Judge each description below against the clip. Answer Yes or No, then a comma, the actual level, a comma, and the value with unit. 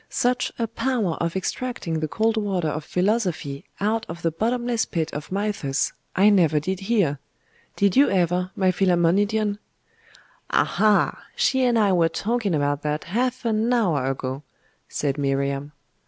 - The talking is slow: No, average, 150 wpm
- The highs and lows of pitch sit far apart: Yes, wide, 5.9 semitones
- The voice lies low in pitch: No, high, 190 Hz